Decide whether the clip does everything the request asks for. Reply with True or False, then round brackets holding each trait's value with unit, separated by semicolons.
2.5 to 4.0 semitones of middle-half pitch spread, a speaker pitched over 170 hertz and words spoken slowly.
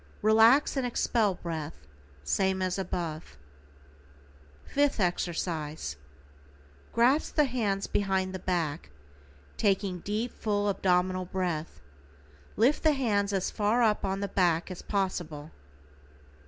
True (3.6 semitones; 190 Hz; 115 wpm)